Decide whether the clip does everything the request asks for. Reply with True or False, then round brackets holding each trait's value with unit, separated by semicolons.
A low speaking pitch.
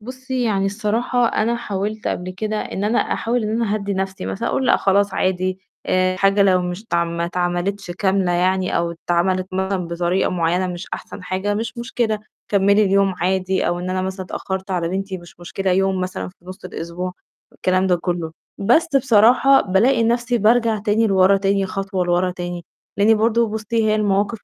False (195 Hz)